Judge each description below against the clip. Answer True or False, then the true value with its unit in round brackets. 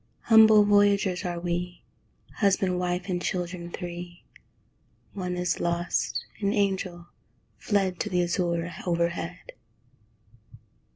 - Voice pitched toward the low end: False (180 Hz)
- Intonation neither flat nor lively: False (2.2 semitones)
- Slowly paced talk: True (105 wpm)